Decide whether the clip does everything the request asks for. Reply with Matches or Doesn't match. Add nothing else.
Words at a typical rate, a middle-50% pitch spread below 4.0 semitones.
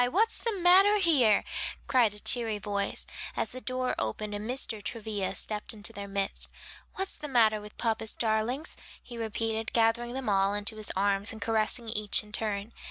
Matches